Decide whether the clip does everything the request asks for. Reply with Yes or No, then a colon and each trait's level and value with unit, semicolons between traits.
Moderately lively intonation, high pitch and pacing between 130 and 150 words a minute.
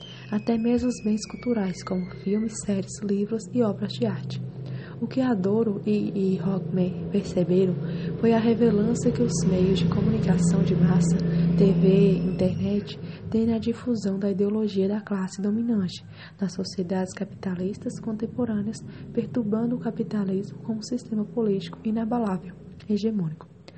Yes: average, 3.4 semitones; high, 200 Hz; slow, 135 wpm